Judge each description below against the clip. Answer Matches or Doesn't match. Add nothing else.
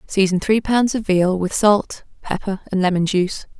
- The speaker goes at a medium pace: Matches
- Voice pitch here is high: Matches